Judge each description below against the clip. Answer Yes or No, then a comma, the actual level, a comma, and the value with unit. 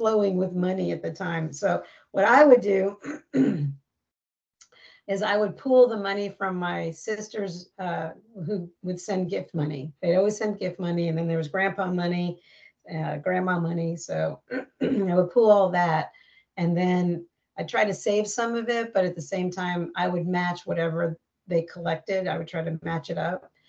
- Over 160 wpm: Yes, average, 185 wpm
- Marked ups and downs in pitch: No, average, 3.0 semitones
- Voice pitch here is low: No, medium, 180 Hz